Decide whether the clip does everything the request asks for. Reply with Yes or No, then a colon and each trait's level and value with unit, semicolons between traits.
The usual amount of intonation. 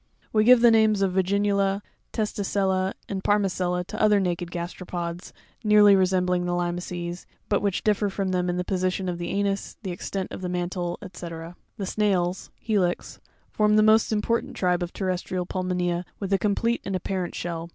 No: narrow, 2.3 semitones